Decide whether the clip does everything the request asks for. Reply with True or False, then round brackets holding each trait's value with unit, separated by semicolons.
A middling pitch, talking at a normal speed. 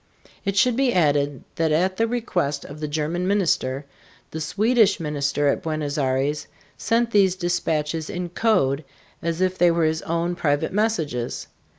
True (165 Hz; 160 wpm)